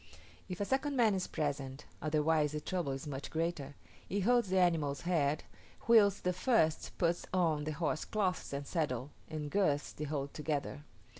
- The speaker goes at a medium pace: Yes, average, 165 wpm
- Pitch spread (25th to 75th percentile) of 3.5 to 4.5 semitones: Yes, average, 4.2 semitones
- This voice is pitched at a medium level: Yes, medium, 155 Hz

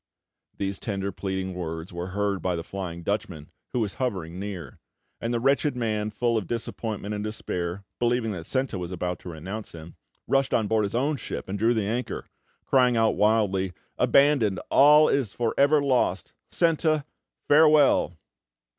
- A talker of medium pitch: No, low, 105 Hz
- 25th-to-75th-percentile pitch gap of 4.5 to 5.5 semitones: Yes, average, 4.9 semitones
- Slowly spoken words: No, average, 165 wpm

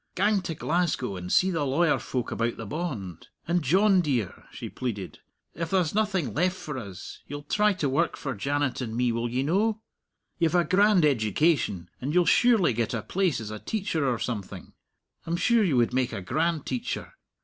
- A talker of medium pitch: Yes, medium, 145 Hz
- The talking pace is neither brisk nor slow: Yes, average, 195 wpm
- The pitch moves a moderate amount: No, wide, 7.2 semitones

